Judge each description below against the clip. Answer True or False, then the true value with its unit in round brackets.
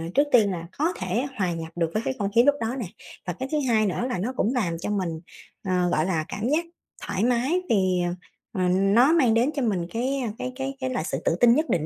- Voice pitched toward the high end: True (220 Hz)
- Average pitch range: False (5.8 semitones)